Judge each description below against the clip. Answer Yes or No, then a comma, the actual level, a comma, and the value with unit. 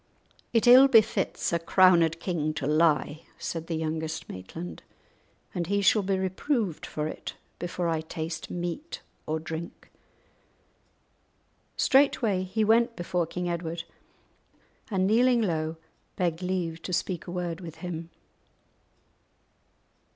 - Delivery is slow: Yes, slow, 125 wpm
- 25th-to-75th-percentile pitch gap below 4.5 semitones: Yes, average, 3.1 semitones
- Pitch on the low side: No, medium, 175 Hz